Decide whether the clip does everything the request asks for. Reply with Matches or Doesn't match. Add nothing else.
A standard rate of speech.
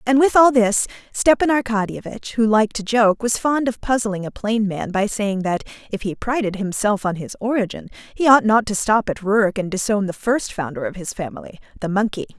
Doesn't match